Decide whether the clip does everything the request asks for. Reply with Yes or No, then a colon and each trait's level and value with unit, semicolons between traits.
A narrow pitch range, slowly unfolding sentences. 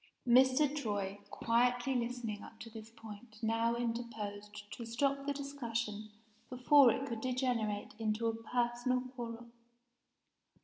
Yes: narrow, 2.2 semitones; slow, 125 wpm